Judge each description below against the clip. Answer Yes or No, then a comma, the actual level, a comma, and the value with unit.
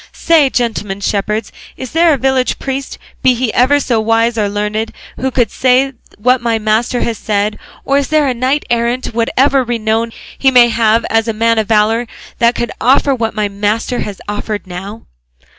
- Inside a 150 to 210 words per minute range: Yes, average, 180 wpm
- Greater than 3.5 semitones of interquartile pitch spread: No, average, 3.1 semitones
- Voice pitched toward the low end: No, high, 230 Hz